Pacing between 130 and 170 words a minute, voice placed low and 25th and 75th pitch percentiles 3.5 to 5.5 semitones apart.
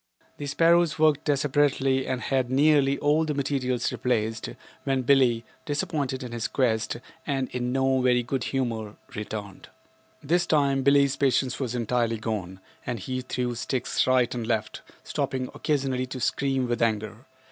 No: average, 155 wpm; low, 130 Hz; average, 2.8 semitones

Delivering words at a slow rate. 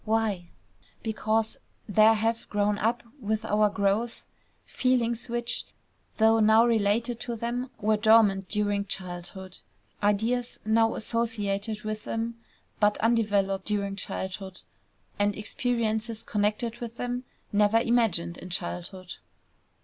Yes: slow, 115 wpm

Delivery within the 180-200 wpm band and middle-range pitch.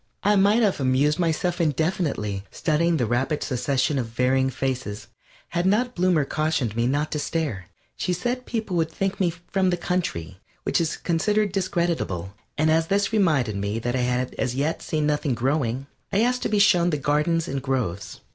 Yes: average, 185 wpm; medium, 155 Hz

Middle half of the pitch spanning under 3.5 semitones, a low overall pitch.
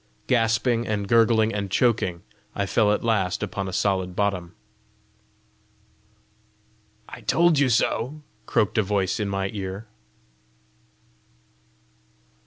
Yes: average, 3.0 semitones; low, 105 Hz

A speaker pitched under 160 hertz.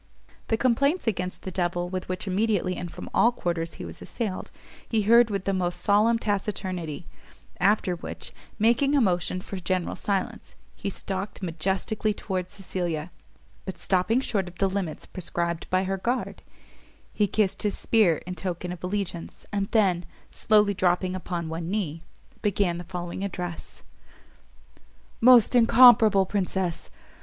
No: high, 190 Hz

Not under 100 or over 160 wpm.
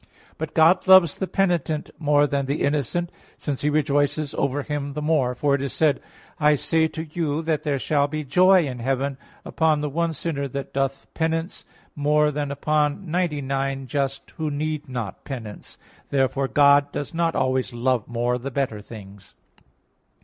No: average, 180 wpm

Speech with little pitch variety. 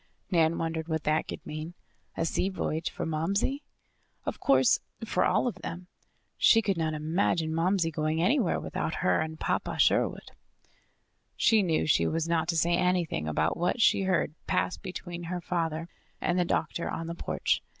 Yes: narrow, 2.3 semitones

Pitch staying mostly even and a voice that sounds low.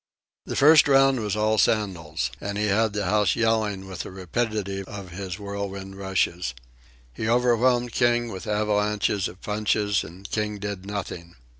Yes: narrow, 2.3 semitones; low, 105 Hz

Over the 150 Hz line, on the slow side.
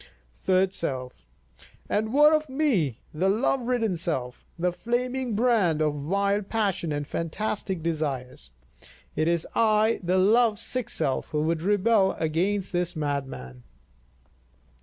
Yes: medium, 185 Hz; slow, 130 wpm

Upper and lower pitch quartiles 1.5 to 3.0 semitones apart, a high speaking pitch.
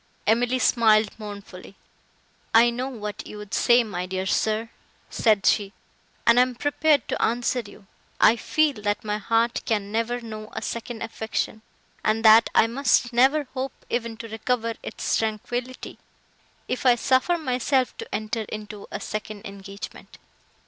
Yes: narrow, 2.5 semitones; high, 225 Hz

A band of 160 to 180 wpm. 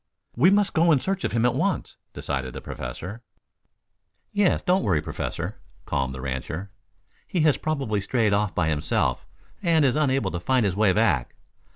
Yes: average, 175 wpm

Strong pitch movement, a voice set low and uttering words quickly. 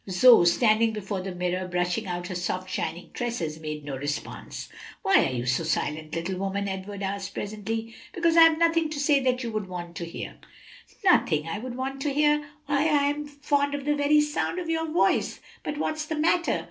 No: wide, 8.6 semitones; high, 220 Hz; fast, 210 wpm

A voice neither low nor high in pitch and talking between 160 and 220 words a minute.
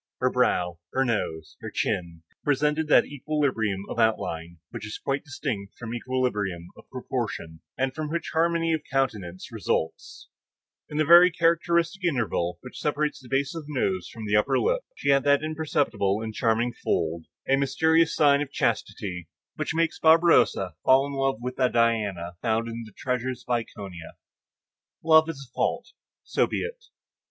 No: low, 130 Hz; average, 165 wpm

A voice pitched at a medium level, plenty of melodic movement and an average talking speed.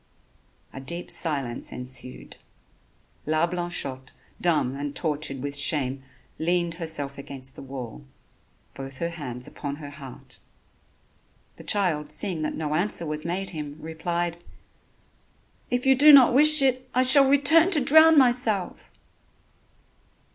No: medium, 160 Hz; wide, 7.4 semitones; slow, 130 wpm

